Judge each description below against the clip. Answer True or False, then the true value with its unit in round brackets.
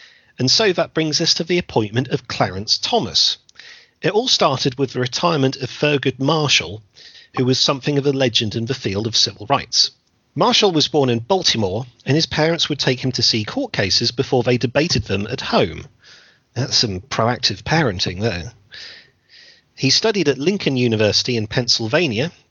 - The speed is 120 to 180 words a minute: True (175 wpm)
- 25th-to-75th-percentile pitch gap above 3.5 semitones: True (4.3 semitones)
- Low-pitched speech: True (130 Hz)